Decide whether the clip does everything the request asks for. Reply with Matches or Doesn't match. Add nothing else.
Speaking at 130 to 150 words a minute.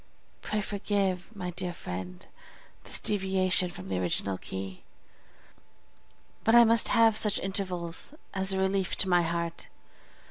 Matches